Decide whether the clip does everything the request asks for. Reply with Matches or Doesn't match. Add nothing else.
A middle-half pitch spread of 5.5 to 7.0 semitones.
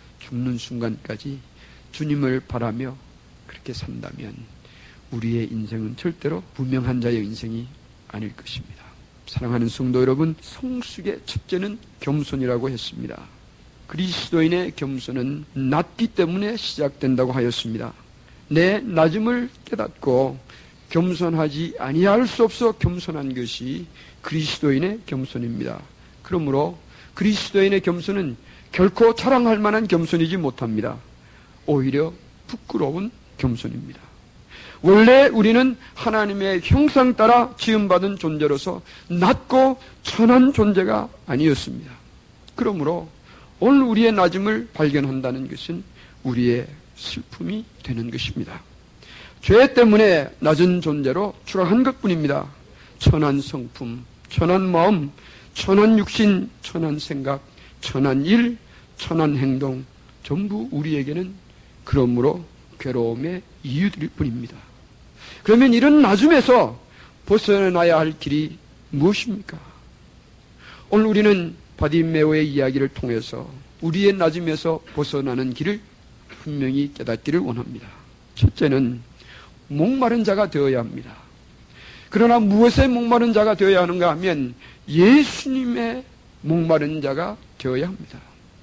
Doesn't match